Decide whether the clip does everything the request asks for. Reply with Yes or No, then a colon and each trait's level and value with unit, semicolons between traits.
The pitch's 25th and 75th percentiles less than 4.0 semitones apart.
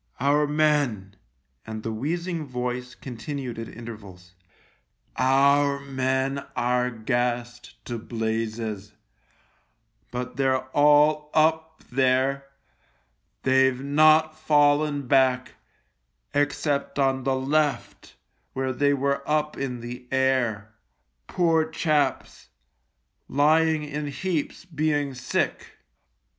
Yes: average, 3.2 semitones